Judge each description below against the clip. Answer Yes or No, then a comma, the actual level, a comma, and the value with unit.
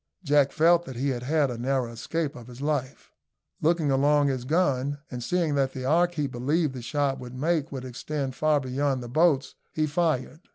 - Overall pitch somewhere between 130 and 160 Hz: Yes, medium, 140 Hz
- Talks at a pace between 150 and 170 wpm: No, average, 200 wpm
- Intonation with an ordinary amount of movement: Yes, average, 3.2 semitones